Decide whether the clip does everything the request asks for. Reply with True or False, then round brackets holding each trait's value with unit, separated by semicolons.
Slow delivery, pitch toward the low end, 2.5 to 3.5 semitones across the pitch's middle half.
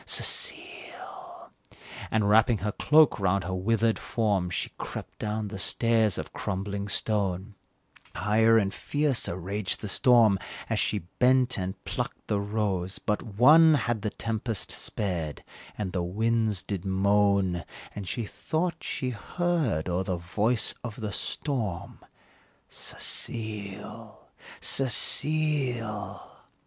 True (125 wpm; 105 Hz; 3.2 semitones)